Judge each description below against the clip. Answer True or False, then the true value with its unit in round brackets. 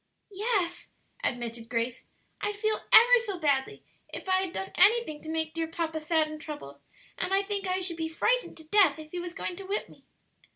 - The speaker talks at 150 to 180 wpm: False (200 wpm)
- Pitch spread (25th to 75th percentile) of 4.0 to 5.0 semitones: True (4.4 semitones)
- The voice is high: True (340 Hz)